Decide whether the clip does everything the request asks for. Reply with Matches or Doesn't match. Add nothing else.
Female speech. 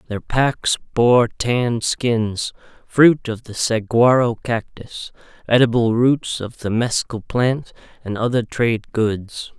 Doesn't match